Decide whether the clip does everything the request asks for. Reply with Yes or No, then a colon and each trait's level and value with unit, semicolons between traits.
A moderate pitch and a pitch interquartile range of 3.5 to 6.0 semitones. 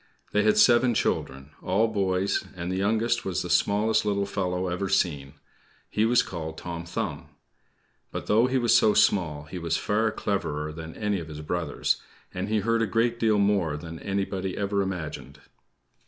No: very low, 95 Hz; average, 4.2 semitones